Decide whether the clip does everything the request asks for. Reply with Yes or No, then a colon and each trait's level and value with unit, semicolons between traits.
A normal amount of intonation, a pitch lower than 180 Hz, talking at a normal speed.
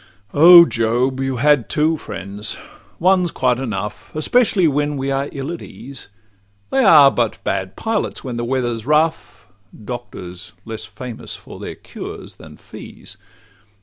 Yes: average, 5.0 semitones; low, 135 Hz; average, 150 wpm